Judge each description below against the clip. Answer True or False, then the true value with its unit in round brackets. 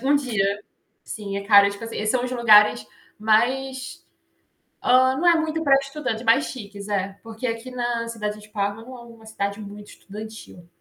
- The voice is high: True (225 Hz)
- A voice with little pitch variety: False (3.7 semitones)